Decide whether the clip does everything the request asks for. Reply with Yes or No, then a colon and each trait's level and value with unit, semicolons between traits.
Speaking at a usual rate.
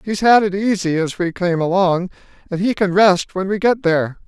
No: fast, 225 wpm